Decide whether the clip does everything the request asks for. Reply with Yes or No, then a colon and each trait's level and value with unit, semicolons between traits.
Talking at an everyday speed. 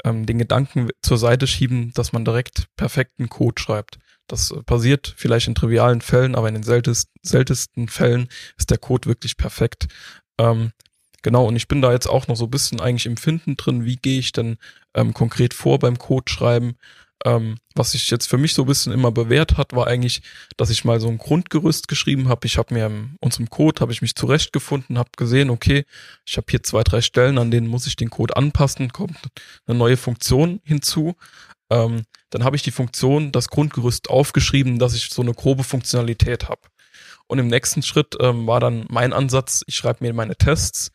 No: fast, 195 wpm